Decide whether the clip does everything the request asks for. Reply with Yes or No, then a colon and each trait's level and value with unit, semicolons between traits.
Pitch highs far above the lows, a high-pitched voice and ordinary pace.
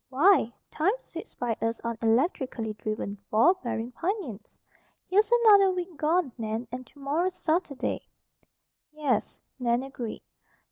No: wide, 7.6 semitones; very high, 270 Hz; slow, 125 wpm